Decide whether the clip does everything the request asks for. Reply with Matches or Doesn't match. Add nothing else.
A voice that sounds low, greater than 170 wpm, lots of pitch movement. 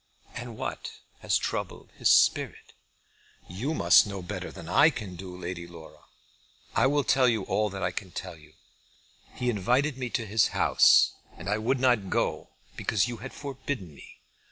Matches